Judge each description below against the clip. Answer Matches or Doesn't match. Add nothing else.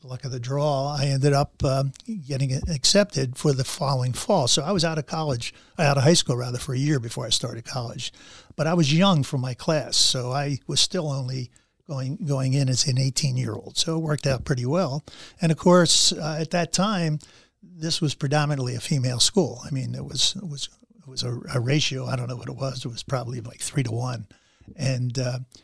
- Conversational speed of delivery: Doesn't match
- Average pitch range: Matches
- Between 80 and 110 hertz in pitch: Doesn't match